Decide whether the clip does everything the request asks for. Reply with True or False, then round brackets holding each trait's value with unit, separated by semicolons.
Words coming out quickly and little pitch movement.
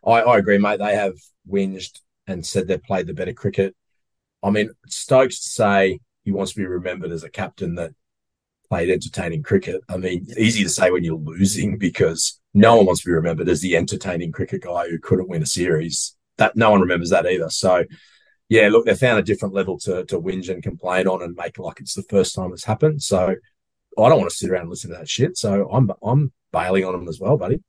False (230 wpm; 3.8 semitones)